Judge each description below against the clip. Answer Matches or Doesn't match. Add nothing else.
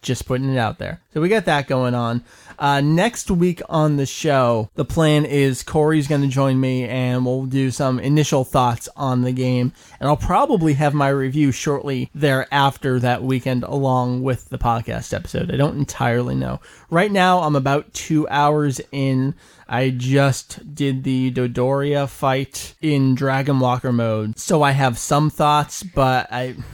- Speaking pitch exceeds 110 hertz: Matches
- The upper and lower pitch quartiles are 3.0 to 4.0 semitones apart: Doesn't match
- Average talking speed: Matches